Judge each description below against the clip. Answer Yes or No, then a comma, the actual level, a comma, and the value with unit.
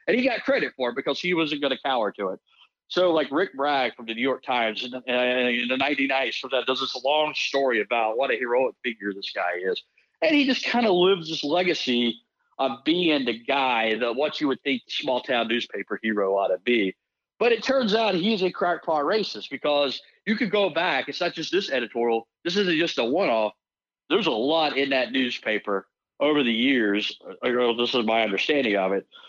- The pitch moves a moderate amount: No, wide, 6.5 semitones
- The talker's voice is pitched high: No, low, 135 Hz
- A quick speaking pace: Yes, fast, 215 wpm